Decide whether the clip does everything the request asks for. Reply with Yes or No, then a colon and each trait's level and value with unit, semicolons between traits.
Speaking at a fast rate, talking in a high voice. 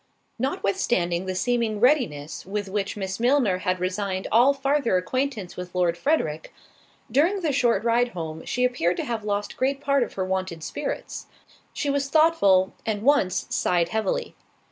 No: average, 160 wpm; high, 210 Hz